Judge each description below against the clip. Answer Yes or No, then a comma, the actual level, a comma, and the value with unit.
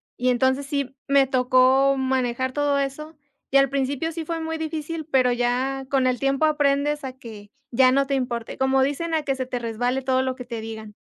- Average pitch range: No, narrow, 1.9 semitones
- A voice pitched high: Yes, very high, 265 Hz